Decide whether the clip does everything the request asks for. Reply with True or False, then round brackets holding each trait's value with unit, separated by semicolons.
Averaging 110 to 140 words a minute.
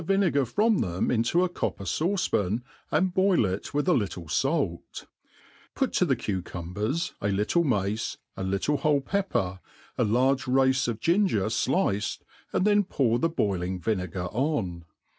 False (155 wpm)